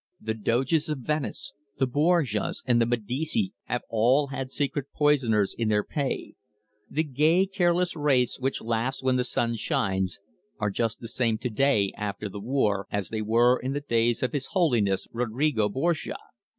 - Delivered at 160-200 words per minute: Yes, average, 170 wpm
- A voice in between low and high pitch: No, low, 125 Hz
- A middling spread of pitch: Yes, average, 4.7 semitones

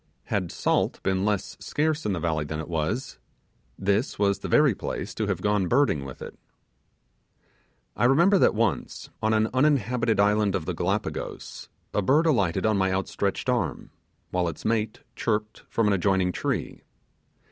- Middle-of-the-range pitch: No, low, 105 Hz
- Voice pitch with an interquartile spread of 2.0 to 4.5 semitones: Yes, average, 4.1 semitones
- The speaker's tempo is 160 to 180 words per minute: Yes, average, 165 wpm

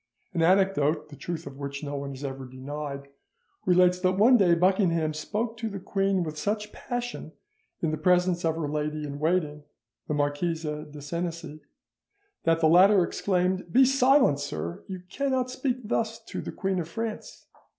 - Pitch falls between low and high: Yes, medium, 170 Hz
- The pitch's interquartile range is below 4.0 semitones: No, average, 4.6 semitones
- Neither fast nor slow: Yes, average, 170 wpm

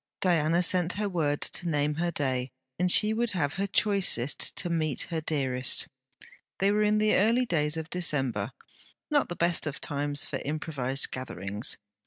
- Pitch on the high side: No, medium, 160 Hz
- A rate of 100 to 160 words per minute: No, average, 170 wpm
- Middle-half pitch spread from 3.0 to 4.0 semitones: No, average, 4.5 semitones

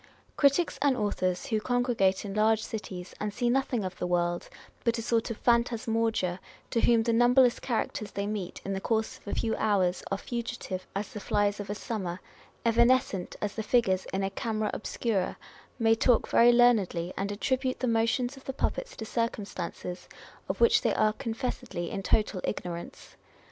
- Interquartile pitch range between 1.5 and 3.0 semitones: No, average, 3.6 semitones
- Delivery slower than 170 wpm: No, average, 180 wpm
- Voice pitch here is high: Yes, high, 220 Hz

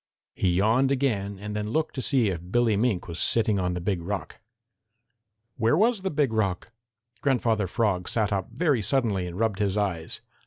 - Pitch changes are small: No, average, 4.5 semitones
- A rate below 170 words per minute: No, average, 185 wpm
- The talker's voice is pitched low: Yes, low, 105 Hz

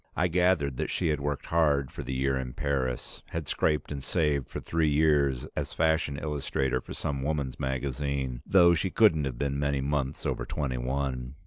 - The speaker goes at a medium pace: Yes, average, 190 wpm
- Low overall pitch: Yes, very low, 70 Hz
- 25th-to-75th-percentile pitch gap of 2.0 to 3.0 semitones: Yes, narrow, 2.6 semitones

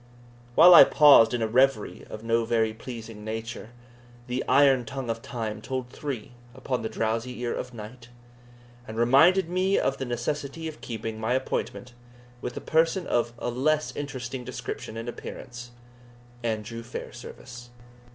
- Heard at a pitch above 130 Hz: No, low, 120 Hz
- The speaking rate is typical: Yes, average, 150 wpm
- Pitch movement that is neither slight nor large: Yes, average, 3.1 semitones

